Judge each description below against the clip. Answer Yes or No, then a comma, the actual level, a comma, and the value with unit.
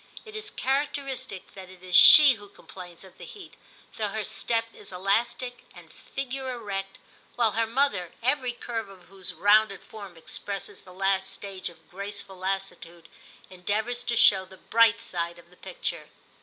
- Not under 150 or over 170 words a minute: Yes, average, 165 wpm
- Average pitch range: Yes, average, 4.2 semitones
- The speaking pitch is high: Yes, high, 200 Hz